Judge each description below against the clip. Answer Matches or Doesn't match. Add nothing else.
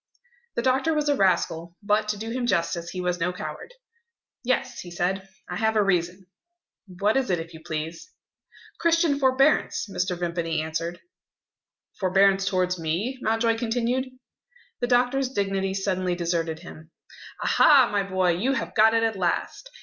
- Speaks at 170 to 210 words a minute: Doesn't match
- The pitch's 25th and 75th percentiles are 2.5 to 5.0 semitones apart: Doesn't match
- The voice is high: Matches